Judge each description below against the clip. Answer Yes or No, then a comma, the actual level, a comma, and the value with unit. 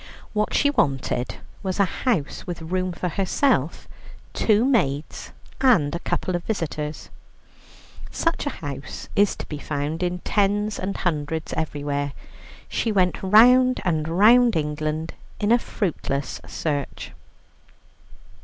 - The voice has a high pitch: No, medium, 180 Hz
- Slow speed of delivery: Yes, slow, 125 wpm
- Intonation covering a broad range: Yes, wide, 5.9 semitones